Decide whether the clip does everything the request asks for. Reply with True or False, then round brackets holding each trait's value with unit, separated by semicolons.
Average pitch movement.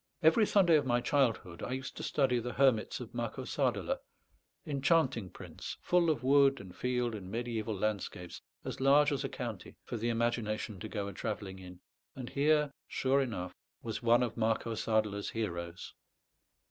True (4.2 semitones)